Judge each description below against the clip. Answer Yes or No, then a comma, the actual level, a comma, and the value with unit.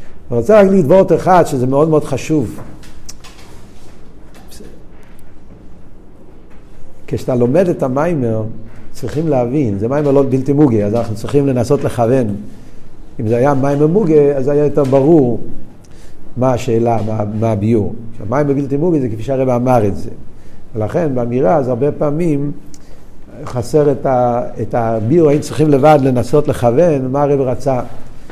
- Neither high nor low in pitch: No, low, 130 Hz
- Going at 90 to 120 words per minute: No, average, 140 wpm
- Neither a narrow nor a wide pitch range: Yes, average, 4.1 semitones